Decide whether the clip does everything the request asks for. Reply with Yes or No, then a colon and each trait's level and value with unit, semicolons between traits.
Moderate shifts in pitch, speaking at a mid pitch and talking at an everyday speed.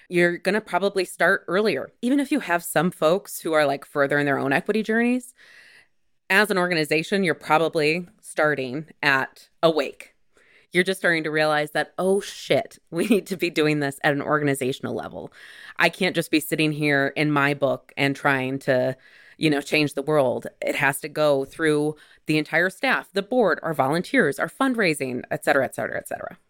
Yes: average, 4.1 semitones; medium, 155 Hz; average, 190 wpm